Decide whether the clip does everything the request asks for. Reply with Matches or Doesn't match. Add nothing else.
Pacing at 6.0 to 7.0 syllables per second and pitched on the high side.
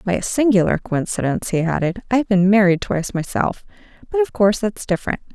Matches